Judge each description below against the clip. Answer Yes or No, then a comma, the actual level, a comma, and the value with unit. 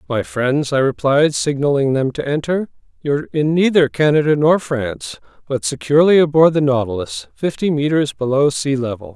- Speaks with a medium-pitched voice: Yes, medium, 145 Hz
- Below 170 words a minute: Yes, average, 155 wpm